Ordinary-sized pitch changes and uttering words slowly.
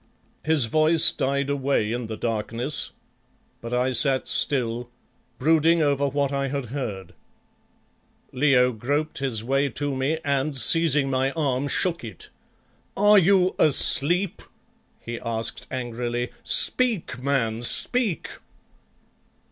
Yes: average, 3.9 semitones; slow, 115 wpm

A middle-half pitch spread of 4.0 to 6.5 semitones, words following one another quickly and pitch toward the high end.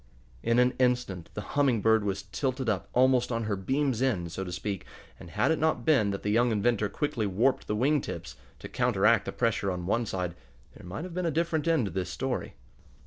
No: average, 4.8 semitones; fast, 220 wpm; low, 115 Hz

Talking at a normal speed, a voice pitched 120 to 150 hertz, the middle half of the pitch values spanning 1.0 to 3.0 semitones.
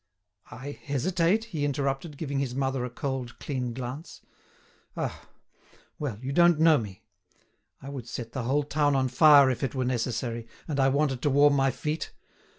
Yes: average, 170 wpm; low, 135 Hz; narrow, 2.6 semitones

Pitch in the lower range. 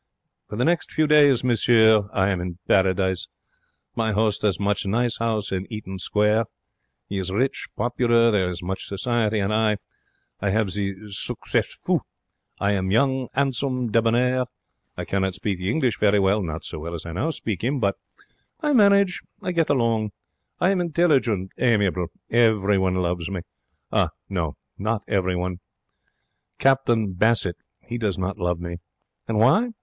Yes: low, 105 Hz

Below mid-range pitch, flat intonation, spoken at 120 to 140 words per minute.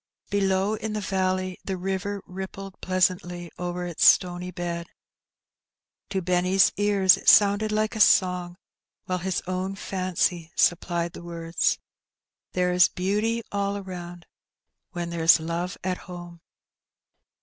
No: medium, 185 Hz; narrow, 1.8 semitones; slow, 135 wpm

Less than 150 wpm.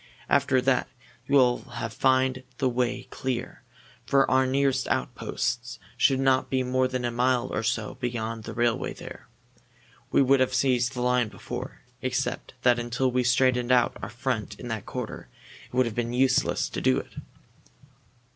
No: average, 165 wpm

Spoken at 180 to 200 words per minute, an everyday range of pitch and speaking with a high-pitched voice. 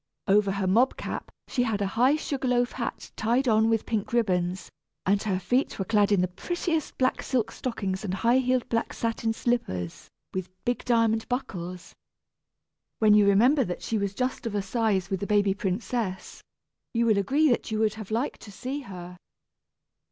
Yes: average, 185 wpm; average, 3.9 semitones; high, 220 Hz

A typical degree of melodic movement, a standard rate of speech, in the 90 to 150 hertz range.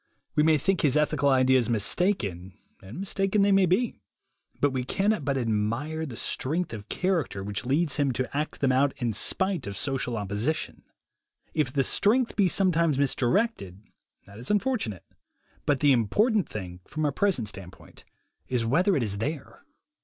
No: wide, 7.9 semitones; average, 170 wpm; medium, 140 Hz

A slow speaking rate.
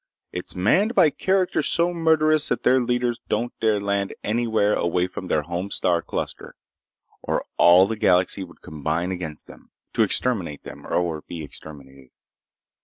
No: average, 155 wpm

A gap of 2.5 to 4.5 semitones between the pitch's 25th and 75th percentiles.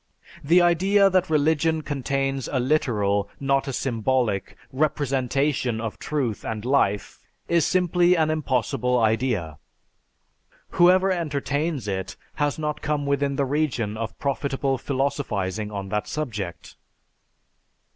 No: average, 5.1 semitones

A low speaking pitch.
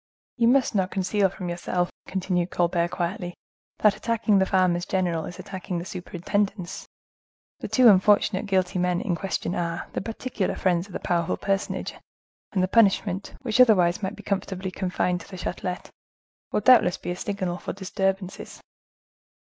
No: medium, 185 Hz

